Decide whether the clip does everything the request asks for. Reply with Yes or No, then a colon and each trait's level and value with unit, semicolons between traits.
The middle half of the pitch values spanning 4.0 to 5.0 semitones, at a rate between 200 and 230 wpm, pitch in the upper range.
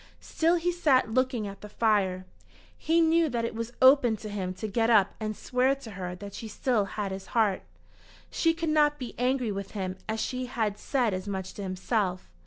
Yes: average, 4.6 semitones; fast, 205 wpm; high, 220 Hz